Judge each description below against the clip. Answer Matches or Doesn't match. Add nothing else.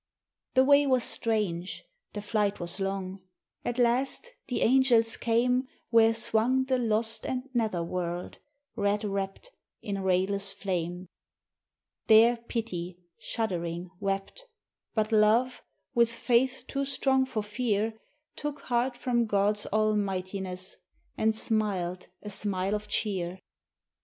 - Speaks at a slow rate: Matches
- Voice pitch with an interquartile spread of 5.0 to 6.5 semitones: Doesn't match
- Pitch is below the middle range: Doesn't match